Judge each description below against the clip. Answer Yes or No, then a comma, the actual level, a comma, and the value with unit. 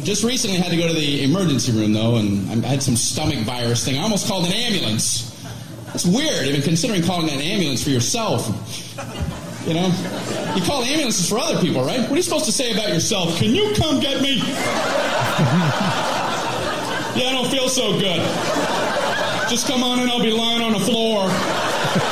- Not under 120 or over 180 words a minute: No, average, 195 wpm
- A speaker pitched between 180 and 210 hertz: Yes, medium, 185 Hz